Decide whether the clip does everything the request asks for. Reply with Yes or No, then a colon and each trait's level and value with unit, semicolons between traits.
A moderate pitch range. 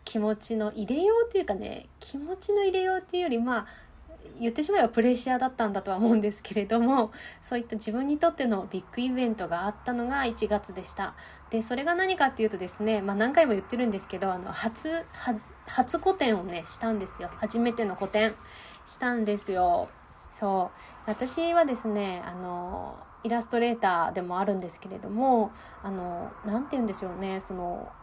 Yes: average, 4.3 semitones